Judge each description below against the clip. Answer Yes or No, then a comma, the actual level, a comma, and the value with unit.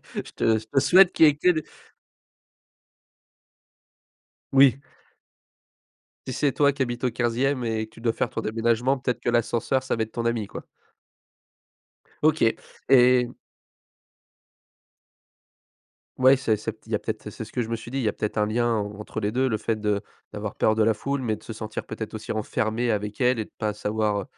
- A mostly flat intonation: No, average, 3.0 semitones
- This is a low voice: Yes, low, 115 Hz